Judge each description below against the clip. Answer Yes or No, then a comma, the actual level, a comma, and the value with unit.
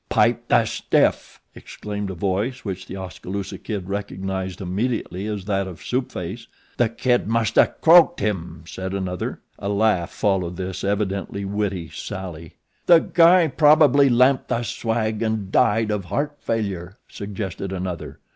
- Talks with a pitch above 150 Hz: No, low, 100 Hz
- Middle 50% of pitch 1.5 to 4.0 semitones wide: Yes, average, 3.4 semitones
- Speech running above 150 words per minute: No, average, 145 wpm